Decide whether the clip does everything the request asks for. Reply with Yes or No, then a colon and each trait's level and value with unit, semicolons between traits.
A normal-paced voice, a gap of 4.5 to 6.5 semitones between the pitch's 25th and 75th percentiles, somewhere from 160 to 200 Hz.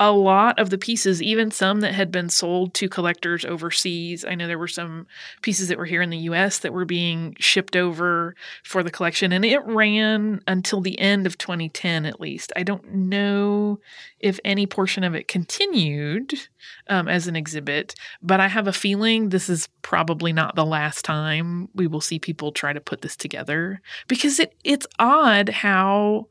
No: average, 190 wpm; average, 3.0 semitones; medium, 185 Hz